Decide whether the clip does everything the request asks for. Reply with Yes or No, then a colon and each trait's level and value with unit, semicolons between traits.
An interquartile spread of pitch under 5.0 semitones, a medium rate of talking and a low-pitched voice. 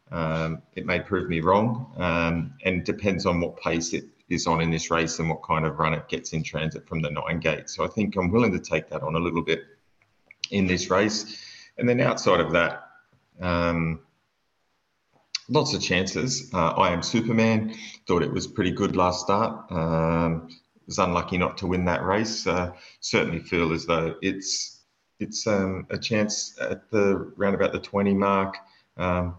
Yes: average, 3.1 semitones; average, 190 wpm; very low, 90 Hz